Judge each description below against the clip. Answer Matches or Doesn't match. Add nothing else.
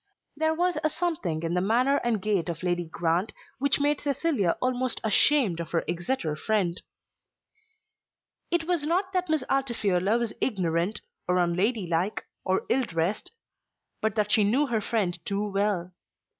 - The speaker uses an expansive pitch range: Matches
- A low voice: Doesn't match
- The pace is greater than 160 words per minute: Doesn't match